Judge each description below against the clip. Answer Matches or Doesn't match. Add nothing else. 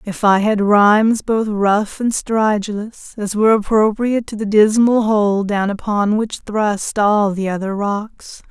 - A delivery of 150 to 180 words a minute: Matches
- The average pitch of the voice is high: Matches